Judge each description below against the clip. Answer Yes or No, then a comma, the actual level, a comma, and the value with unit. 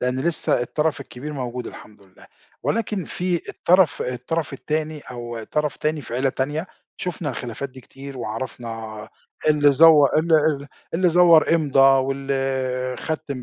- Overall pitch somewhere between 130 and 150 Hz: Yes, medium, 140 Hz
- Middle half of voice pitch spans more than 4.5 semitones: No, average, 3.8 semitones